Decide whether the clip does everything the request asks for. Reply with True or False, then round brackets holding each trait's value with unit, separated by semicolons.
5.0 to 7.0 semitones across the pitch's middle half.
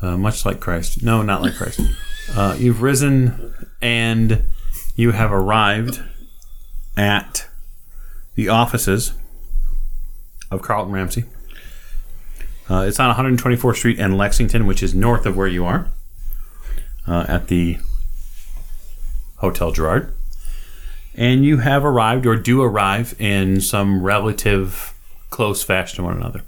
True (5.3 semitones)